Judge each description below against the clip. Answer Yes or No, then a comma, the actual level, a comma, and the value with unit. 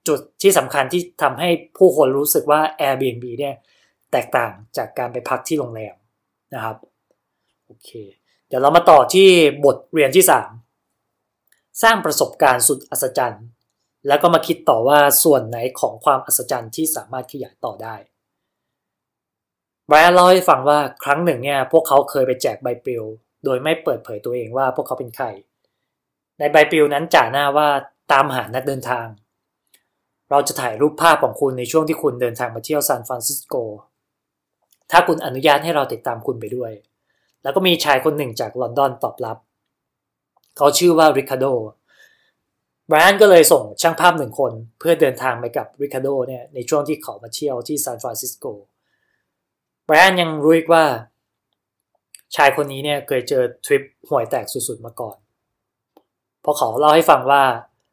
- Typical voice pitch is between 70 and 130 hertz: No, medium, 140 Hz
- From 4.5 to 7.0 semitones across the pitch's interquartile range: No, average, 4.1 semitones